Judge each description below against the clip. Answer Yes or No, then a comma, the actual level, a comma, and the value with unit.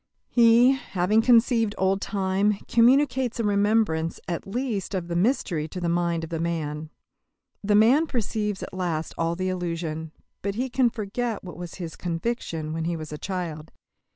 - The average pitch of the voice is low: No, high, 190 Hz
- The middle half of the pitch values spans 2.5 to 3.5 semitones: No, average, 5.3 semitones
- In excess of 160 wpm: Yes, average, 170 wpm